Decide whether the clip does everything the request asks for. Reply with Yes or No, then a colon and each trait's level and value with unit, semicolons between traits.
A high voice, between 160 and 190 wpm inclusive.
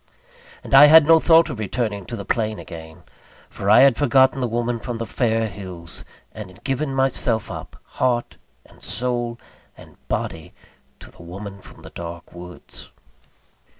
No: low, 115 Hz; average, 165 wpm